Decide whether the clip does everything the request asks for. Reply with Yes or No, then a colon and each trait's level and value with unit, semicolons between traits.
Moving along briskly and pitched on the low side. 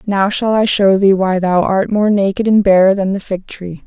No: fast, 250 wpm; high, 195 Hz